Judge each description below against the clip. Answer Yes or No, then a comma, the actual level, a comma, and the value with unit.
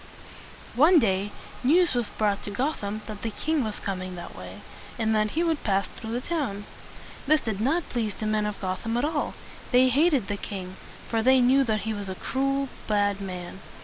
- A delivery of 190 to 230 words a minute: Yes, average, 200 wpm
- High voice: Yes, high, 220 Hz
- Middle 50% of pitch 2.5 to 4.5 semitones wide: No, average, 5.0 semitones